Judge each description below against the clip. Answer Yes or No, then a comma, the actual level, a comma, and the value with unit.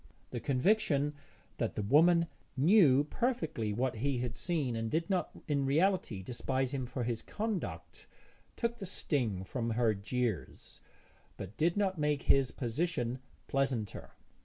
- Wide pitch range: Yes, wide, 6.0 semitones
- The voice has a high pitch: No, low, 135 Hz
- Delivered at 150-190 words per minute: No, average, 140 wpm